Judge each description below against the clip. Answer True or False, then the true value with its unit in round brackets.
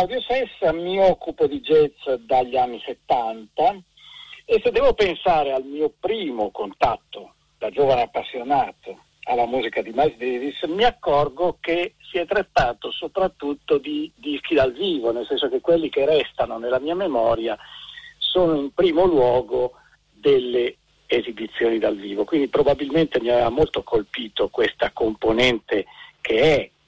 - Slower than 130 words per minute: False (145 wpm)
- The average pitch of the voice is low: False (185 Hz)